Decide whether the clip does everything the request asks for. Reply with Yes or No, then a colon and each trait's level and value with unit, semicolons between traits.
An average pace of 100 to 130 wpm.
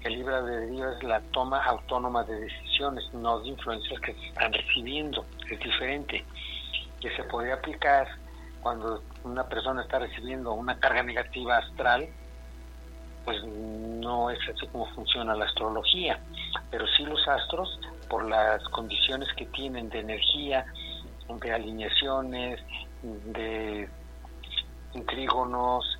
Yes: slow, 125 wpm